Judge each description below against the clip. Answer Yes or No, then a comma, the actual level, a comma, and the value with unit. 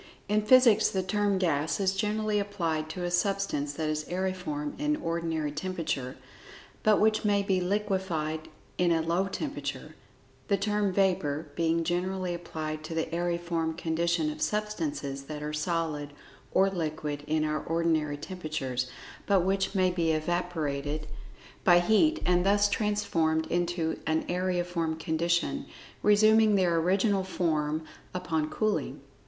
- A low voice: No, medium, 175 Hz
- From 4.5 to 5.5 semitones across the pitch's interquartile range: No, average, 3.7 semitones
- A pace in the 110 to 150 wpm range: Yes, average, 140 wpm